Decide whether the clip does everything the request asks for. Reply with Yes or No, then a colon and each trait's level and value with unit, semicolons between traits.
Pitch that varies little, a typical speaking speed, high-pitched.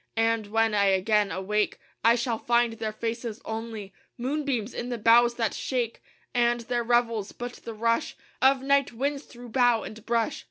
Yes: narrow, 1.7 semitones; average, 170 wpm; high, 230 Hz